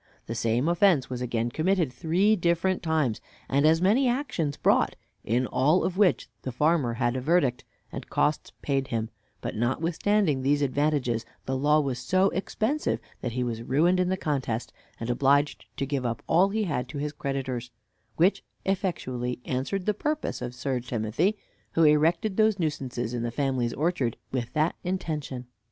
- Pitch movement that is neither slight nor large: No, wide, 5.9 semitones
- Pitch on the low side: No, medium, 145 Hz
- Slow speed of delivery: No, average, 170 wpm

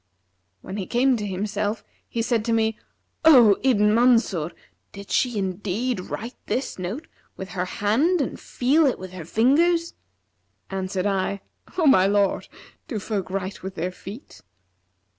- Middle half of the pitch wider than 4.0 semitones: Yes, average, 4.6 semitones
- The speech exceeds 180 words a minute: No, average, 150 wpm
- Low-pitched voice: No, high, 210 Hz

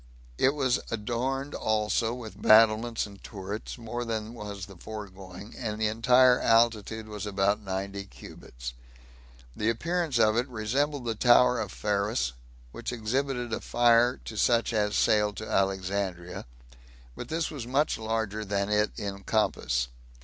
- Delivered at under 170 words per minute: Yes, average, 140 wpm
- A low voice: Yes, low, 110 Hz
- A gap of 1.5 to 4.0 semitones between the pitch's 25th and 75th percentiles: Yes, average, 3.0 semitones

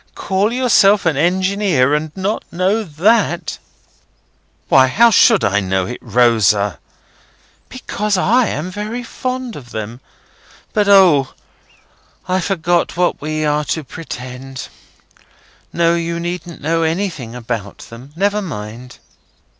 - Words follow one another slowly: Yes, slow, 125 wpm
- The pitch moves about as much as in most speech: No, wide, 7.5 semitones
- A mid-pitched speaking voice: Yes, medium, 170 Hz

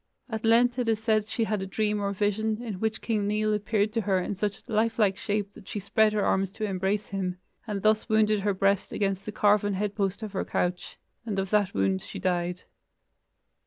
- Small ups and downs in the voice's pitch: Yes, narrow, 1.9 semitones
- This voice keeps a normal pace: No, fast, 220 wpm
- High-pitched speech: Yes, high, 205 Hz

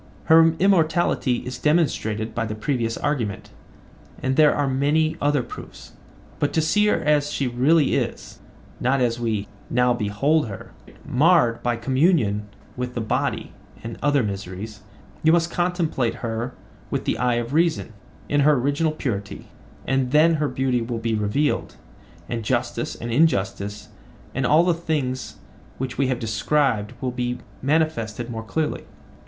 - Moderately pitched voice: No, low, 130 Hz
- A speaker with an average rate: Yes, average, 150 wpm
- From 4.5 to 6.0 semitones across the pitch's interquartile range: Yes, average, 4.8 semitones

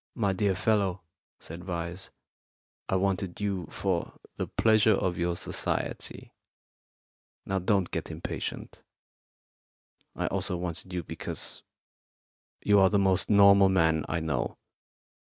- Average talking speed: No, slow, 120 wpm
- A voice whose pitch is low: Yes, very low, 95 Hz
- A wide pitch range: No, narrow, 2.4 semitones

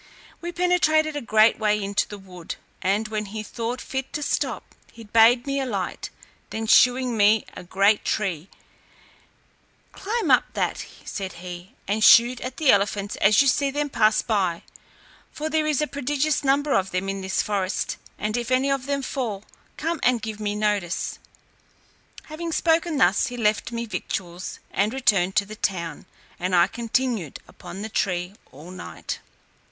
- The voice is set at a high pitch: Yes, high, 220 Hz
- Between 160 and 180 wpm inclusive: Yes, average, 170 wpm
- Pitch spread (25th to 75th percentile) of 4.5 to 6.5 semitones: Yes, wide, 5.5 semitones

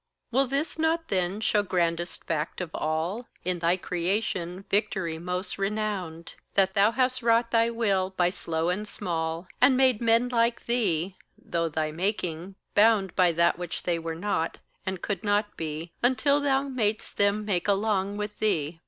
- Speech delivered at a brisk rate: No, average, 165 wpm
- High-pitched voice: Yes, high, 195 Hz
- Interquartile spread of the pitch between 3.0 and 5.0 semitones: Yes, average, 4.7 semitones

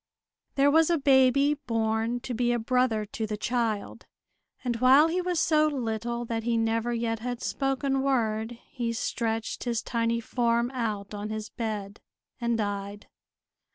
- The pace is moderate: Yes, average, 155 wpm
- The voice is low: No, high, 235 Hz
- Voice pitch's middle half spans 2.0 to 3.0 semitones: Yes, narrow, 2.6 semitones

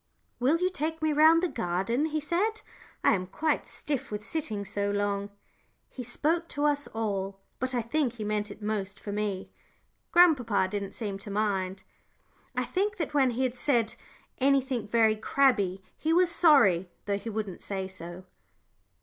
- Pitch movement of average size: No, wide, 6.7 semitones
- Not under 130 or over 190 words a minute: Yes, average, 170 wpm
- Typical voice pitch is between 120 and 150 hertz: No, high, 230 Hz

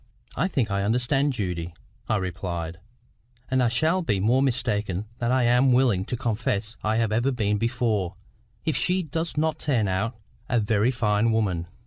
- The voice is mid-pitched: No, low, 115 Hz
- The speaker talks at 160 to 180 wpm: Yes, average, 170 wpm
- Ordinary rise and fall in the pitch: Yes, average, 4.2 semitones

